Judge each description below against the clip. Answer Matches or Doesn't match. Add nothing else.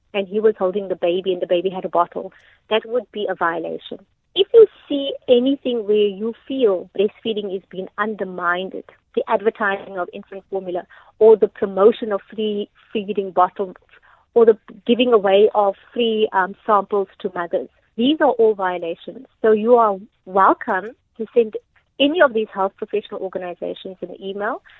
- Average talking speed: Matches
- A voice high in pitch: Matches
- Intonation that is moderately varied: Matches